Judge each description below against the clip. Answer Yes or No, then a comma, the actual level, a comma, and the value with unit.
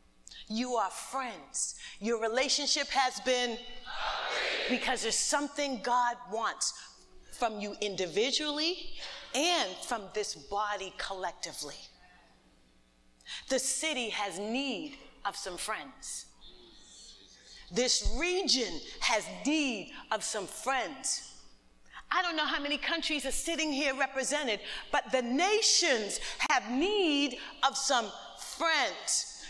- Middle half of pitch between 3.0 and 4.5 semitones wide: No, wide, 5.4 semitones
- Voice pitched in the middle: No, very high, 255 Hz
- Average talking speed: No, slow, 105 wpm